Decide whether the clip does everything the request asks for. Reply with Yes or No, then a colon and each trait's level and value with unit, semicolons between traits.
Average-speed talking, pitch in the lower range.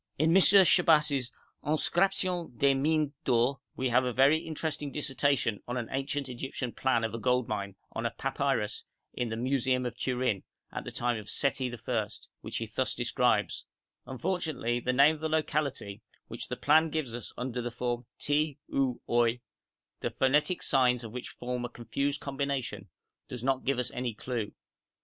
Yes: average, 175 wpm; low, 130 Hz